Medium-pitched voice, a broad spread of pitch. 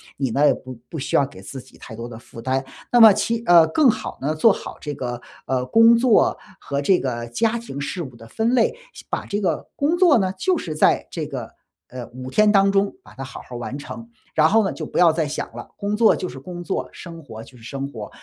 Yes: medium, 160 Hz; wide, 8.4 semitones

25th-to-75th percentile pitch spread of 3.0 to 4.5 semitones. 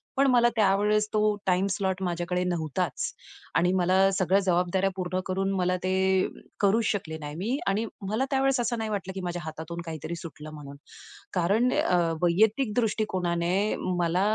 Yes: average, 3.3 semitones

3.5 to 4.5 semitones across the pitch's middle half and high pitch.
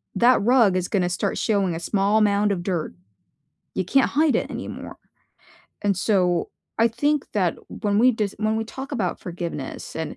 Yes: average, 3.8 semitones; high, 205 Hz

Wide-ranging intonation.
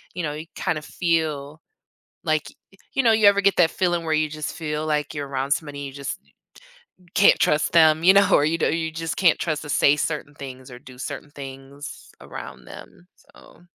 No: narrow, 2.6 semitones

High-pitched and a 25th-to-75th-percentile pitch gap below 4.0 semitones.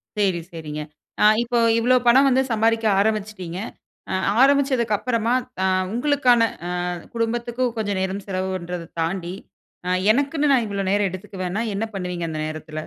No: high, 210 Hz; average, 4.7 semitones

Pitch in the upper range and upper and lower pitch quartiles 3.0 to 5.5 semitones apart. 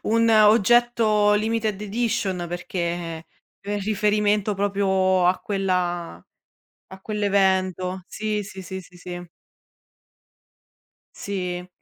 No: high, 195 Hz; narrow, 2.6 semitones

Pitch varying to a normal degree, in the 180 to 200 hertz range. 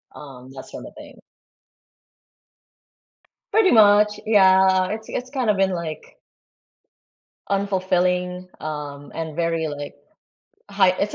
Yes: average, 4.4 semitones; medium, 185 Hz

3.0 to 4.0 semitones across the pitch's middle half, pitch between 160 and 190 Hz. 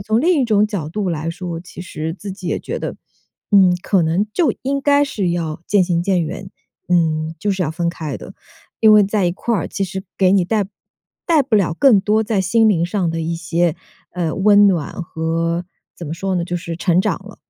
Yes: average, 3.7 semitones; medium, 185 Hz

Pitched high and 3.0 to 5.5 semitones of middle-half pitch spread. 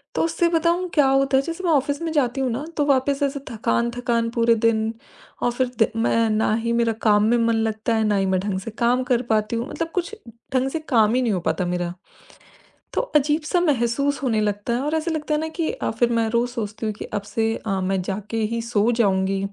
Yes: high, 235 Hz; average, 4.5 semitones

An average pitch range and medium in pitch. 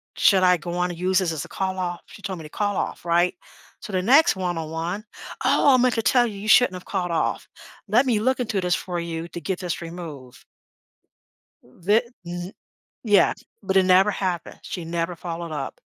Yes: average, 3.0 semitones; medium, 180 Hz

